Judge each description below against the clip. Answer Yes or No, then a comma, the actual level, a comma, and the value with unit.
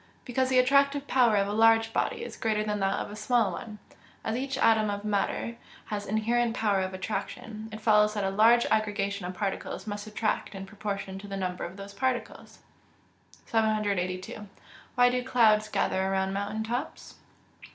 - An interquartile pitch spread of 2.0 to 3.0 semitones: Yes, narrow, 2.5 semitones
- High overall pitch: Yes, high, 215 Hz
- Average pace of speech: Yes, average, 180 wpm